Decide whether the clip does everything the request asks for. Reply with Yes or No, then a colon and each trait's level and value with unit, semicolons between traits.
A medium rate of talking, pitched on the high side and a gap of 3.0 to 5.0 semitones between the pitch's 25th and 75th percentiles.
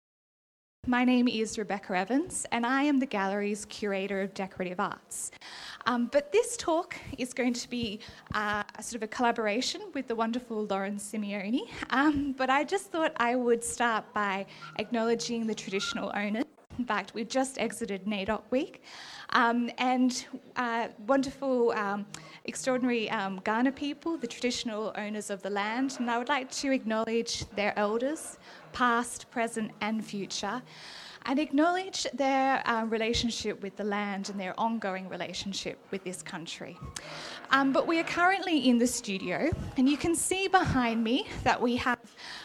Yes: average, 160 wpm; high, 235 Hz; average, 4.1 semitones